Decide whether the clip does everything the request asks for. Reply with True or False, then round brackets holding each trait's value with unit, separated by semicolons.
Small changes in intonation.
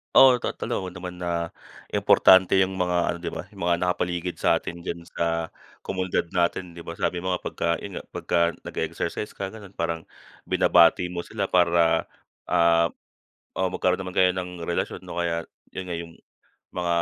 True (1.5 semitones)